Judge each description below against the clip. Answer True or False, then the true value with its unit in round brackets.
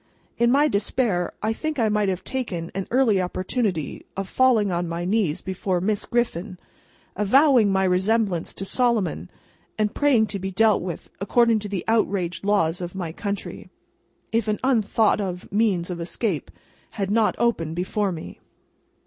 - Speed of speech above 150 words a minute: True (160 wpm)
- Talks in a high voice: True (200 Hz)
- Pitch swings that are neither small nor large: True (3.8 semitones)